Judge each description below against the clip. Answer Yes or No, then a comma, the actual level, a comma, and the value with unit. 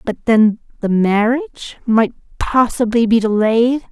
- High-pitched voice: Yes, high, 230 Hz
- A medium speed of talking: No, slow, 125 wpm